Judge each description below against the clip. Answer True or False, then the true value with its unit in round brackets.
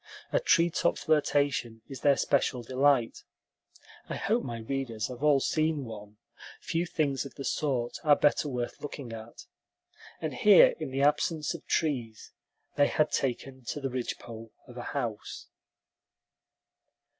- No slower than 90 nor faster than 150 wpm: True (145 wpm)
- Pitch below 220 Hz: True (135 Hz)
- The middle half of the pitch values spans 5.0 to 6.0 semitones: False (3.8 semitones)